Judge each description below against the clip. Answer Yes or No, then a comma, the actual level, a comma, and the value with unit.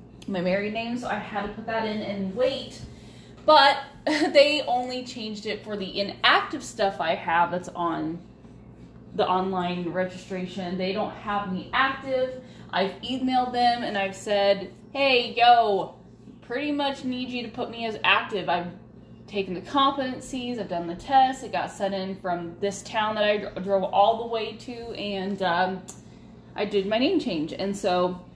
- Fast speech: No, average, 170 wpm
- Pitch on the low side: No, high, 210 Hz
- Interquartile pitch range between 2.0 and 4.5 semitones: No, average, 5.0 semitones